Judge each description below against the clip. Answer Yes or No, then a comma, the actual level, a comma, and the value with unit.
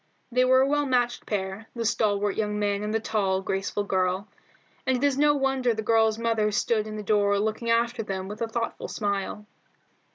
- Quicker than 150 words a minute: Yes, average, 200 wpm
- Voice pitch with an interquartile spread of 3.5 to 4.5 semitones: No, average, 2.7 semitones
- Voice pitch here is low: No, high, 215 Hz